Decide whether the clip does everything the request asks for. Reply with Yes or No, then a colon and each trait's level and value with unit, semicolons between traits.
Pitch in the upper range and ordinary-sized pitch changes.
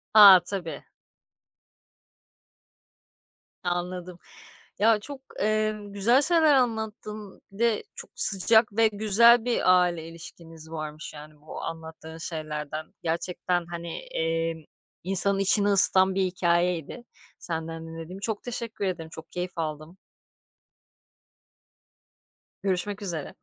No: medium, 180 Hz; average, 4.4 semitones